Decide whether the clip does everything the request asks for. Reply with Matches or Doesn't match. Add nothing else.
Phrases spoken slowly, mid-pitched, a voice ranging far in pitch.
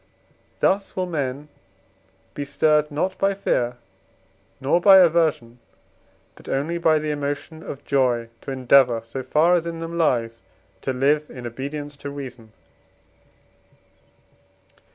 Doesn't match